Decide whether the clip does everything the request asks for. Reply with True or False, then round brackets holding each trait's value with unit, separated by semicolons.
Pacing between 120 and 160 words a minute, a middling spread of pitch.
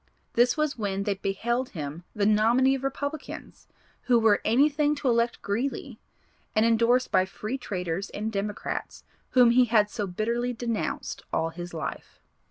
True (155 wpm; 3.8 semitones)